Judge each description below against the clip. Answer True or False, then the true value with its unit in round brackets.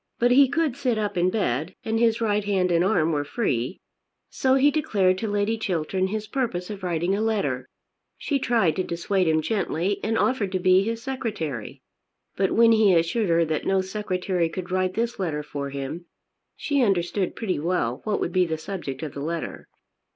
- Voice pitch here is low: False (190 Hz)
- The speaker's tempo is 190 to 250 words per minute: True (195 wpm)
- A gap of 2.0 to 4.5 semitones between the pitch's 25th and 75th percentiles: False (4.9 semitones)